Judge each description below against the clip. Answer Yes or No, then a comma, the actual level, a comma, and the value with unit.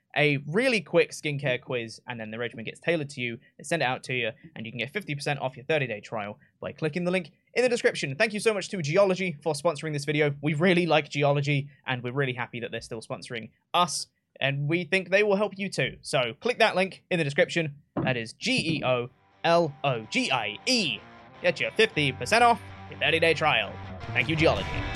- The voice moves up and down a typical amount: No, wide, 6.1 semitones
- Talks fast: Yes, fast, 230 wpm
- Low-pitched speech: No, medium, 150 Hz